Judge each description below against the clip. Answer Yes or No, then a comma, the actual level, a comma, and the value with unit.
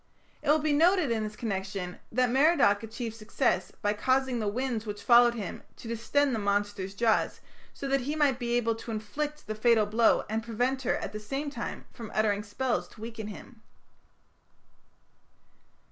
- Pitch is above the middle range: Yes, high, 230 Hz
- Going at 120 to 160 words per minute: No, average, 175 wpm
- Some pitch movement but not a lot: Yes, average, 3.7 semitones